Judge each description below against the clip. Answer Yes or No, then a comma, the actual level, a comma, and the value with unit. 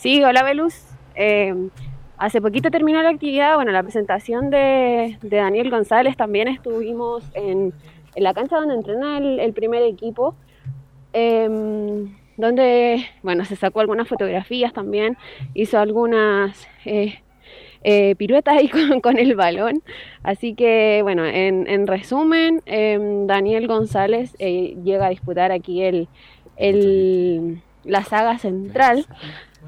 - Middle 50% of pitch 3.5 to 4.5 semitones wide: Yes, average, 4.1 semitones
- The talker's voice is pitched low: No, high, 215 Hz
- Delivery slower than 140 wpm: Yes, average, 130 wpm